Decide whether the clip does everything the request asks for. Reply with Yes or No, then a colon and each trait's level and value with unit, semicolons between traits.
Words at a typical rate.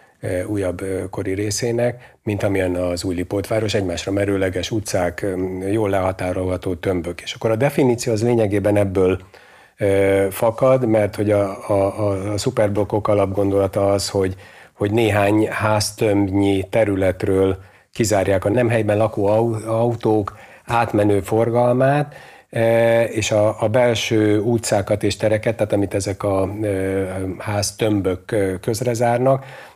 Yes: average, 115 wpm